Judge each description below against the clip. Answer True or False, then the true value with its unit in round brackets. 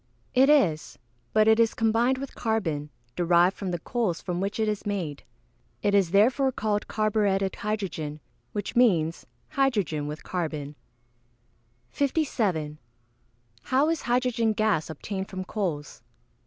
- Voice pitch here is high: True (205 Hz)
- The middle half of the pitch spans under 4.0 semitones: False (5.1 semitones)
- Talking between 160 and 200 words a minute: False (135 wpm)